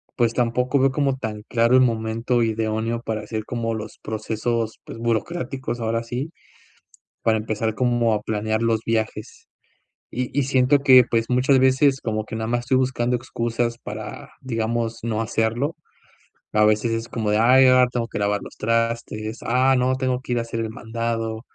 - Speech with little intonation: Yes, narrow, 2.2 semitones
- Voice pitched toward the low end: Yes, low, 115 Hz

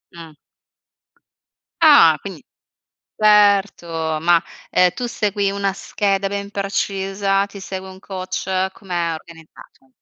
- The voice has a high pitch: Yes, high, 195 Hz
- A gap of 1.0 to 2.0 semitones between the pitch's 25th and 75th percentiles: No, narrow, 2.5 semitones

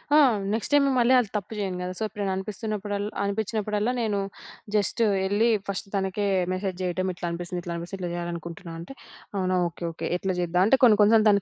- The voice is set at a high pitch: Yes, high, 200 Hz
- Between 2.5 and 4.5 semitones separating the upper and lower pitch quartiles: Yes, average, 2.9 semitones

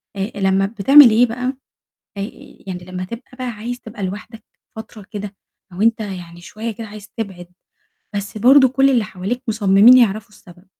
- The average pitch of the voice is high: Yes, high, 215 Hz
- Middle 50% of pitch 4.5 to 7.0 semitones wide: No, average, 3.3 semitones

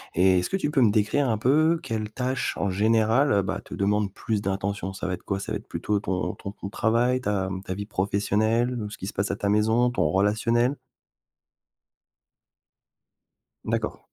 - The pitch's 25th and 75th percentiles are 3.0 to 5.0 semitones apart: Yes, average, 3.3 semitones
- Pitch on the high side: No, low, 105 Hz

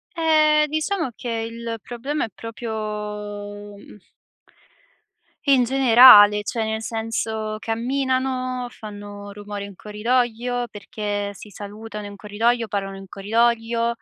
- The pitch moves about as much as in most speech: Yes, average, 3.0 semitones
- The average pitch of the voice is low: No, high, 225 Hz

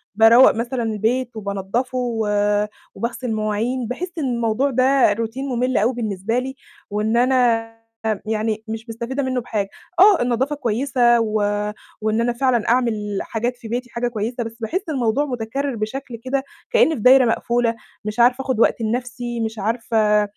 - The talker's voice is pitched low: No, high, 235 Hz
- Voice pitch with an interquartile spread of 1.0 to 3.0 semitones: Yes, narrow, 2.5 semitones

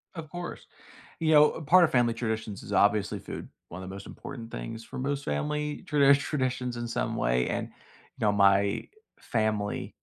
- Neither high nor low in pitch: No, low, 115 Hz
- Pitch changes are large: Yes, wide, 6.0 semitones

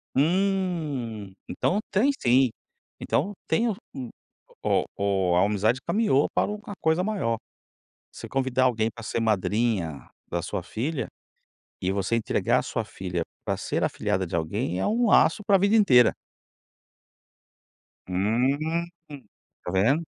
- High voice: No, low, 125 Hz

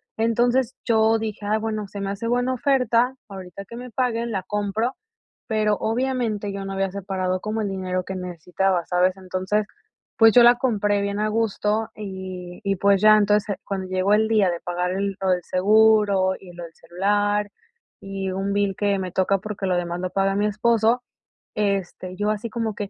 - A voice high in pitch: Yes, high, 205 Hz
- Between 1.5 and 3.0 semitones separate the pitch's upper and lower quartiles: Yes, average, 2.7 semitones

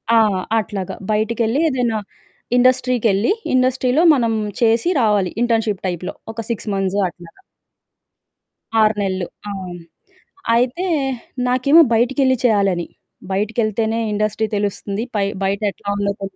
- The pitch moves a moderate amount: Yes, average, 3.5 semitones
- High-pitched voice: Yes, high, 220 Hz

